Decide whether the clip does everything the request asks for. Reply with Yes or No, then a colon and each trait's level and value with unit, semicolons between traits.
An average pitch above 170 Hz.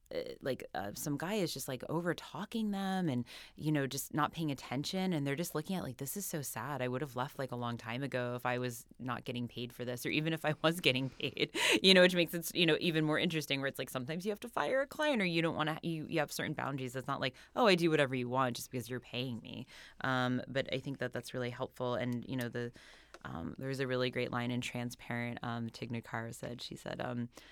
No: low, 135 Hz